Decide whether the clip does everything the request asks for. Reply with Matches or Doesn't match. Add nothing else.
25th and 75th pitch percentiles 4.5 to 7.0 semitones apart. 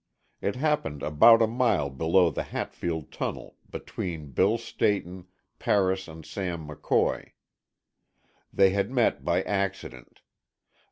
Doesn't match